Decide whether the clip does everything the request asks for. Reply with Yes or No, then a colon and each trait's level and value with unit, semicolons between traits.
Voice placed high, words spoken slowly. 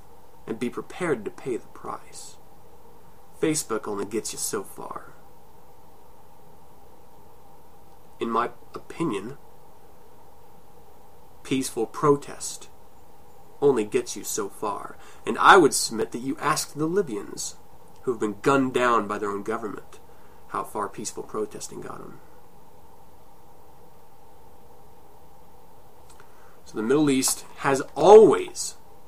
Yes: high, 205 Hz; slow, 110 wpm